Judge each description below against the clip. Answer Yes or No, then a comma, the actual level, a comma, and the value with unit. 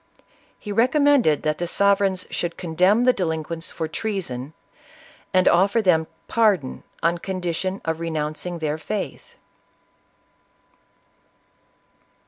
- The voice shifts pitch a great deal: No, average, 3.9 semitones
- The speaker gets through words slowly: Yes, slow, 110 wpm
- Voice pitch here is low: No, medium, 180 Hz